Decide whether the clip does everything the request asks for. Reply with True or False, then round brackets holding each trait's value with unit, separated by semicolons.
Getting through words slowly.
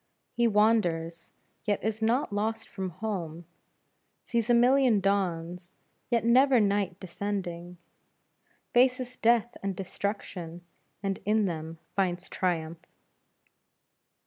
True (105 wpm)